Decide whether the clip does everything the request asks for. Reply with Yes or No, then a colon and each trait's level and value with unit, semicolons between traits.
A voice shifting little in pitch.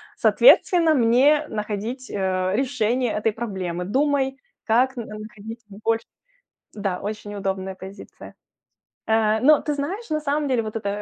No: average, 4.6 semitones